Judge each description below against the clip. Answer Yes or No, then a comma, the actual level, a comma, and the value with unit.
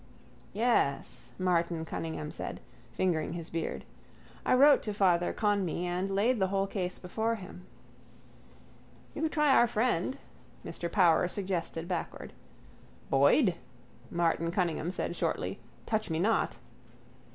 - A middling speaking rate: No, slow, 125 wpm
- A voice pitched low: No, medium, 180 Hz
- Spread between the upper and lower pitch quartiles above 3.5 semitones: Yes, average, 4.0 semitones